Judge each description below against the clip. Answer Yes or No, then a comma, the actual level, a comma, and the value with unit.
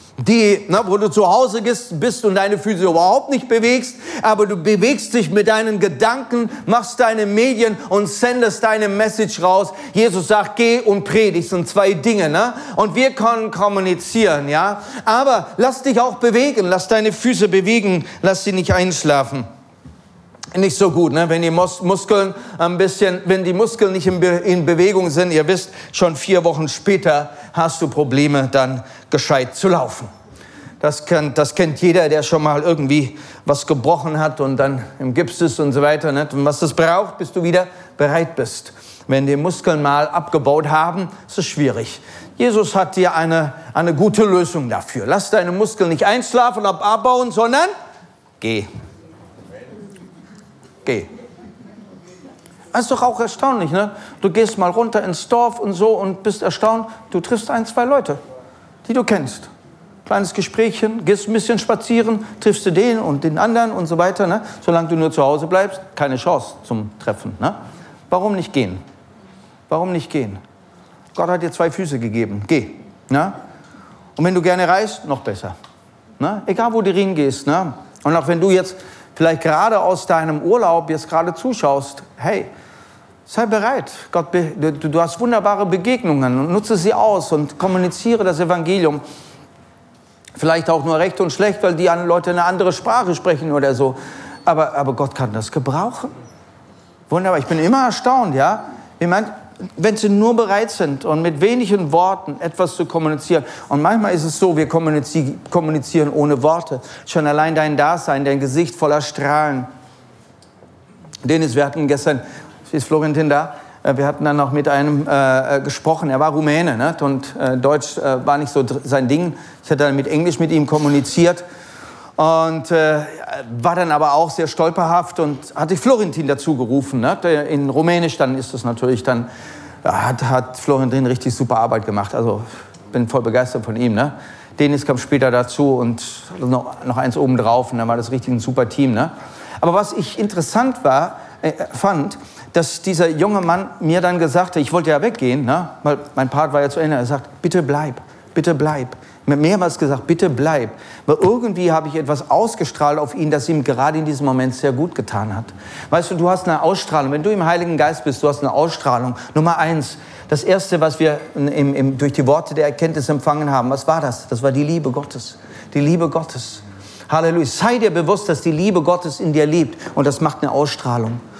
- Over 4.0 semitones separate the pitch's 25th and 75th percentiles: Yes, average, 5.3 semitones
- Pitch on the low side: No, medium, 165 Hz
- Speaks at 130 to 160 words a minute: No, average, 180 wpm